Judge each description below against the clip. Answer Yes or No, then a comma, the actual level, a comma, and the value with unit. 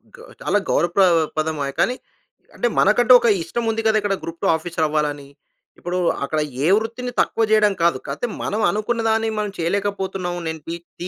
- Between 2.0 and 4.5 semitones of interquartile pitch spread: No, average, 5.1 semitones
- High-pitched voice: Yes, high, 195 Hz